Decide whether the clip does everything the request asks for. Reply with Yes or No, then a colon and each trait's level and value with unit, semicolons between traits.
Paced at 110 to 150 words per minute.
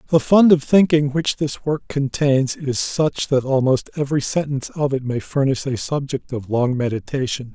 No: average, 185 wpm